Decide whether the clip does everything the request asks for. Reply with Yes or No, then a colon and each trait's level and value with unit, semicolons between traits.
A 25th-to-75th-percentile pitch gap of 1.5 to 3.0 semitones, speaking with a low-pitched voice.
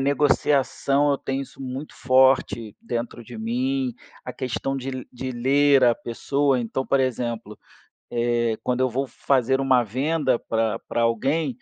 Yes: narrow, 2.6 semitones; low, 130 Hz